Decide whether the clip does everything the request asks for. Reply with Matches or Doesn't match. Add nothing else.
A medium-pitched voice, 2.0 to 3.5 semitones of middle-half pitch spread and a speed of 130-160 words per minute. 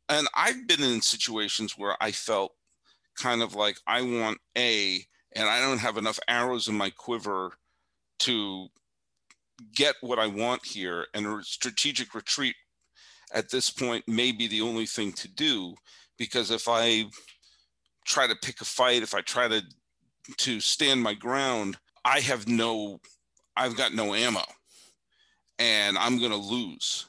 Doesn't match